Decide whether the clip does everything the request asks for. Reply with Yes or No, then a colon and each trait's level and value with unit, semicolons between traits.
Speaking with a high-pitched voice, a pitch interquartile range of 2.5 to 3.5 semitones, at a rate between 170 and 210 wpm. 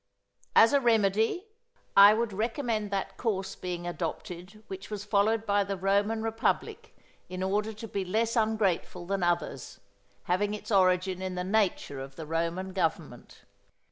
No: high, 195 Hz; average, 3.2 semitones; average, 150 wpm